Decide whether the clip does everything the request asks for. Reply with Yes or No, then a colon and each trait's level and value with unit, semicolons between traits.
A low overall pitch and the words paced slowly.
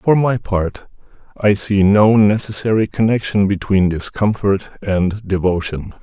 Yes: low, 100 Hz; slow, 120 wpm